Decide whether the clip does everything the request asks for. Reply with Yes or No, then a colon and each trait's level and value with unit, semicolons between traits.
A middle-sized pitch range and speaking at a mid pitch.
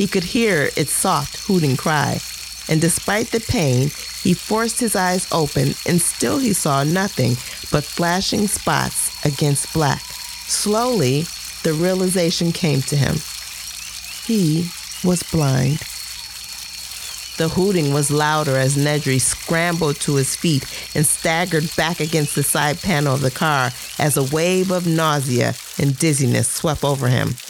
Yes: average, 4.2 semitones; medium, 155 Hz